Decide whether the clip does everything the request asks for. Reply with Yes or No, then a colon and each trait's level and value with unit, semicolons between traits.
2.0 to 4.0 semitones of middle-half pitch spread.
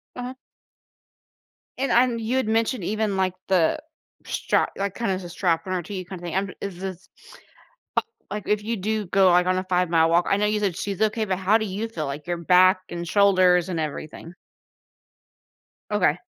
Yes: average, 3.1 semitones